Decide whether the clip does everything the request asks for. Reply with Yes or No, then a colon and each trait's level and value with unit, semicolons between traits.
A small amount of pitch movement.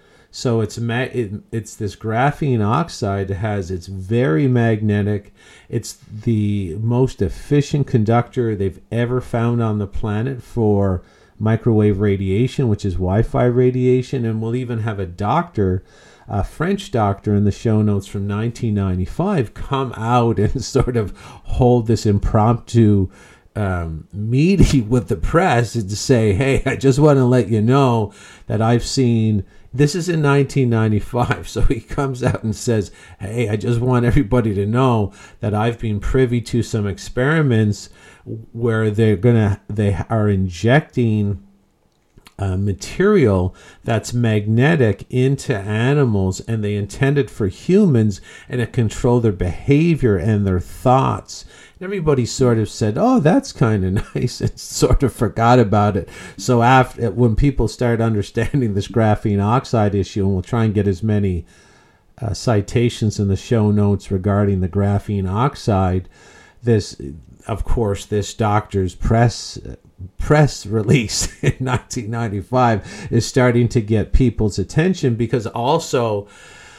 No: average, 3.7 semitones